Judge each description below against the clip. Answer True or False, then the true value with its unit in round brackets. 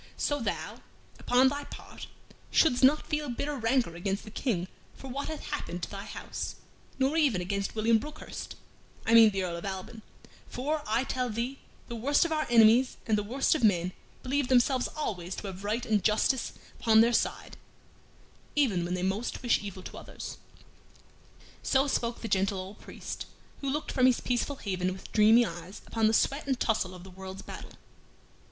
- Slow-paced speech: False (185 wpm)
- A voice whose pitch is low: False (230 Hz)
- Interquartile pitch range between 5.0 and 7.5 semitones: True (5.3 semitones)